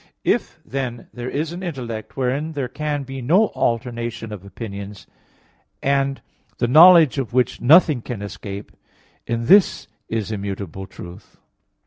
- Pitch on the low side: Yes, low, 120 Hz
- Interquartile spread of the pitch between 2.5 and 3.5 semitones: No, average, 4.8 semitones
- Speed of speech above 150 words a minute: No, slow, 135 wpm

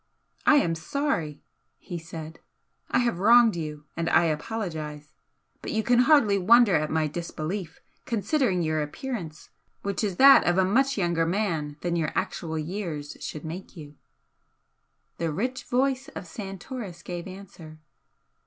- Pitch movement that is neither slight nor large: No, wide, 5.8 semitones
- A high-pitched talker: No, medium, 180 Hz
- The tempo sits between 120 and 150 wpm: Yes, average, 145 wpm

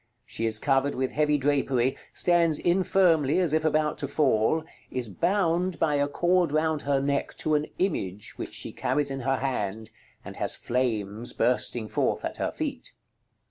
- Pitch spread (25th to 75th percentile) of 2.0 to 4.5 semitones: Yes, average, 4.0 semitones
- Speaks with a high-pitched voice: No, medium, 145 Hz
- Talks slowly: No, average, 170 wpm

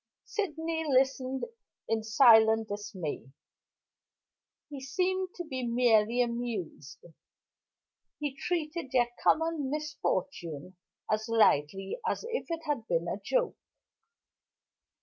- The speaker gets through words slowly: Yes, slow, 100 wpm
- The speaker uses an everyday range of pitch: No, wide, 6.0 semitones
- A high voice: Yes, very high, 255 Hz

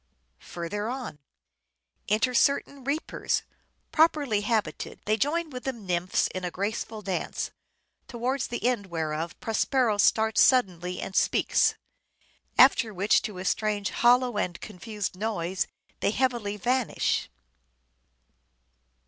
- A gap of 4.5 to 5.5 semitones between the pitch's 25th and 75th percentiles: Yes, average, 5.1 semitones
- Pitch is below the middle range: No, high, 215 Hz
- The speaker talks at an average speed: No, slow, 120 wpm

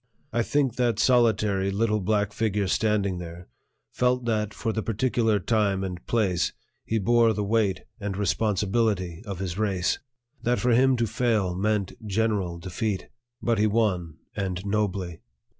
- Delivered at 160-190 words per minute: No, average, 150 wpm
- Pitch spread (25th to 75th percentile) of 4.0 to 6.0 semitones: No, average, 3.0 semitones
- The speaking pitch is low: Yes, low, 105 Hz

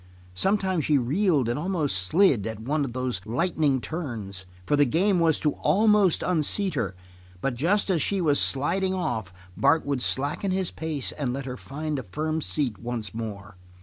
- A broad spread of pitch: Yes, wide, 6.4 semitones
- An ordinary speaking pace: Yes, average, 180 wpm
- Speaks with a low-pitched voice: No, medium, 145 Hz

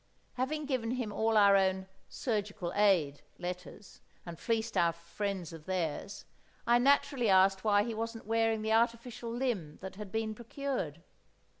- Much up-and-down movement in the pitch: No, average, 3.7 semitones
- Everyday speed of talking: Yes, average, 150 wpm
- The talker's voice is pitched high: Yes, high, 210 Hz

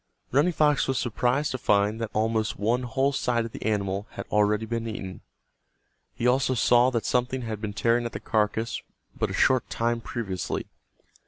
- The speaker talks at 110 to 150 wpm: No, average, 180 wpm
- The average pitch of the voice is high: No, low, 115 Hz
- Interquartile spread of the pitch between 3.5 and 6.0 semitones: No, average, 2.7 semitones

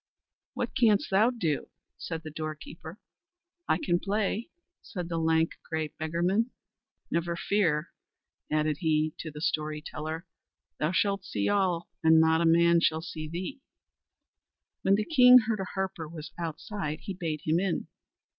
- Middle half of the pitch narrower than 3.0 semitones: No, average, 3.8 semitones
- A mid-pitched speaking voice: Yes, medium, 170 Hz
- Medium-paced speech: Yes, average, 155 wpm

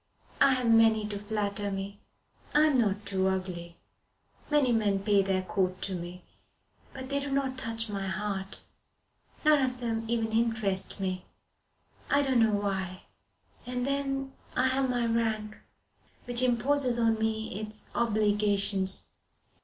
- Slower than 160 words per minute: Yes, average, 145 wpm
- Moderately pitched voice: No, high, 220 Hz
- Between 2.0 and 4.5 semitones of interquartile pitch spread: Yes, average, 4.0 semitones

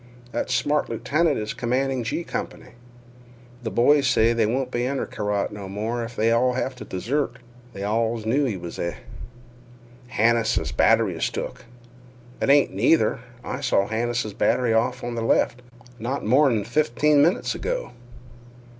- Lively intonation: No, average, 3.4 semitones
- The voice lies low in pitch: Yes, low, 120 Hz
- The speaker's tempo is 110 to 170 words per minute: Yes, average, 155 wpm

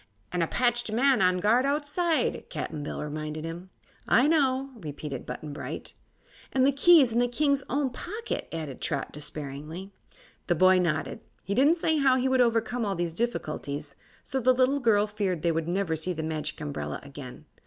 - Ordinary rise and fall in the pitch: No, wide, 8.7 semitones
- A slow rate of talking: No, average, 180 wpm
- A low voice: No, high, 200 Hz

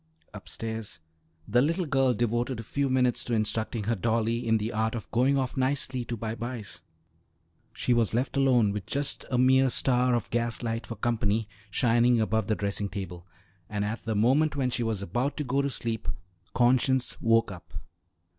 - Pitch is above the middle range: No, low, 120 Hz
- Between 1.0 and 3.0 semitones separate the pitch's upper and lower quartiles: Yes, narrow, 2.5 semitones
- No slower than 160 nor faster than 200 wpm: Yes, average, 185 wpm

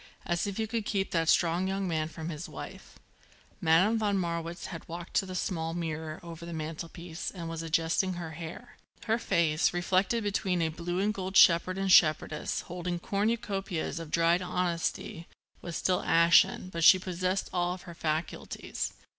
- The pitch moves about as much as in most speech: No, narrow, 2.3 semitones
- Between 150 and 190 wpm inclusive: Yes, average, 170 wpm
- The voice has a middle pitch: Yes, medium, 175 Hz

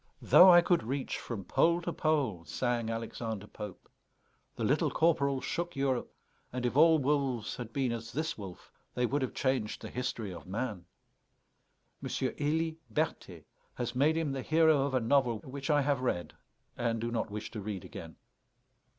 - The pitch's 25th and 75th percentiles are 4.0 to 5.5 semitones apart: Yes, average, 4.5 semitones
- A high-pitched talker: No, low, 130 Hz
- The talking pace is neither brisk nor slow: Yes, average, 175 wpm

